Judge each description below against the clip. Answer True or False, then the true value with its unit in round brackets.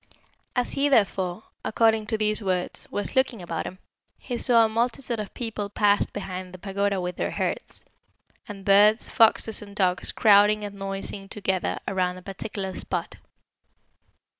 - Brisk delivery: False (155 wpm)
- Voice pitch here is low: False (205 Hz)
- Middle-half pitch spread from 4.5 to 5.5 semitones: False (2.4 semitones)